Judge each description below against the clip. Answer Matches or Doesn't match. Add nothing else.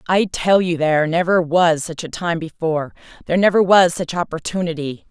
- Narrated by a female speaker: Matches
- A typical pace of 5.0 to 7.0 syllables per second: Matches